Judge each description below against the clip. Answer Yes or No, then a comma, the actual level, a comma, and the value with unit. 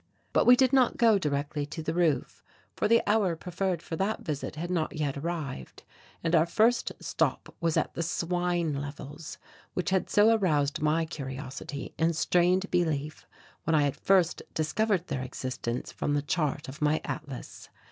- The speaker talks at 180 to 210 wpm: No, average, 170 wpm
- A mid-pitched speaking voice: Yes, medium, 160 Hz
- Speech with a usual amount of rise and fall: Yes, average, 3.8 semitones